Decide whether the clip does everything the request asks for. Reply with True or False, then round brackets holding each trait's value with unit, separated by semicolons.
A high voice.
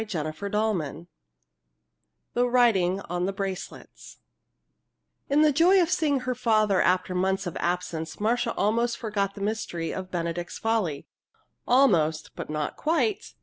True (200 Hz)